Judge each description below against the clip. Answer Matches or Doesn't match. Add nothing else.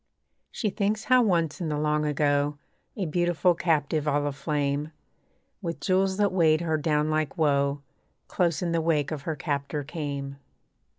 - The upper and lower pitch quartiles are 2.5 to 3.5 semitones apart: Matches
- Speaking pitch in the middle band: Matches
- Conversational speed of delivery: Matches